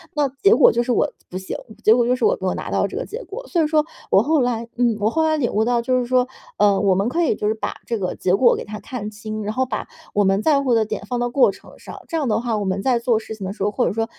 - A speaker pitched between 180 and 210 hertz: No, high, 235 Hz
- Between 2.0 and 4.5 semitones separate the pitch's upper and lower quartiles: Yes, average, 3.7 semitones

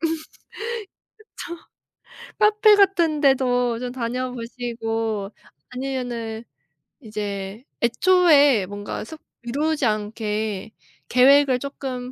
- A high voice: Yes, very high, 250 Hz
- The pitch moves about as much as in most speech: Yes, average, 4.1 semitones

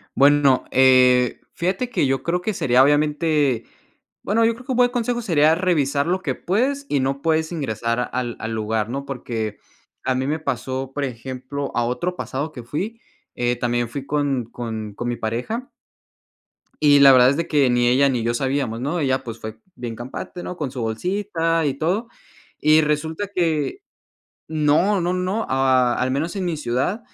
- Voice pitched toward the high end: No, medium, 140 Hz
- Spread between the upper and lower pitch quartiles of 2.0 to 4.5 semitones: No, average, 5.3 semitones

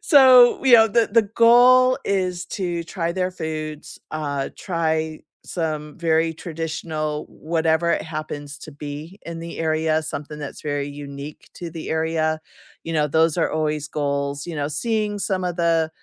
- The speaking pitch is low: No, medium, 160 Hz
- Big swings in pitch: No, average, 2.9 semitones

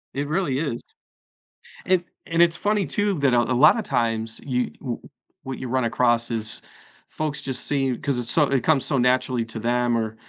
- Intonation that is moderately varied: Yes, average, 3.8 semitones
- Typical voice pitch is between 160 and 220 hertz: No, low, 130 Hz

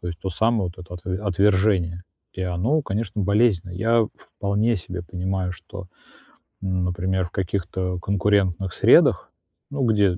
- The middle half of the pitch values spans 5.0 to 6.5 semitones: No, narrow, 2.4 semitones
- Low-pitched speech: Yes, very low, 95 Hz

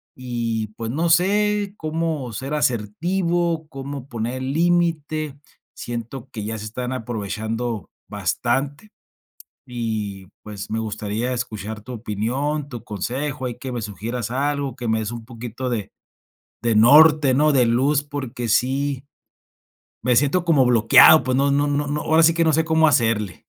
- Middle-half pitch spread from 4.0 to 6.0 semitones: Yes, average, 4.6 semitones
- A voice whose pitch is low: Yes, low, 130 Hz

